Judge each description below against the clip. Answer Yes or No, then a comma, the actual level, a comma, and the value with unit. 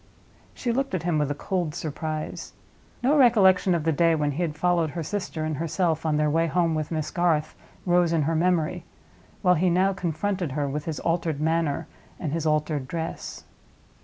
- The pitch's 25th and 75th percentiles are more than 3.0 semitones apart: No, narrow, 2.6 semitones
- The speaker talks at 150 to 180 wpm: No, average, 190 wpm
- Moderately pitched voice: Yes, medium, 165 Hz